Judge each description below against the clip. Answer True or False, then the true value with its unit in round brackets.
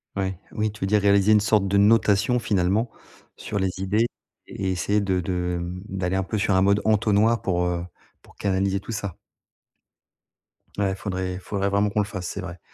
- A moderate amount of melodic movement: False (1.9 semitones)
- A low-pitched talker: True (100 Hz)